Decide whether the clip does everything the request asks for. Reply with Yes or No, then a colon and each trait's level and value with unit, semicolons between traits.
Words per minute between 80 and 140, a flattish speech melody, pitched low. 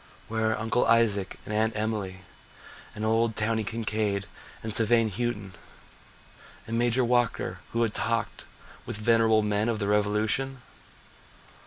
Yes: slow, 135 wpm; narrow, 1.7 semitones; low, 110 Hz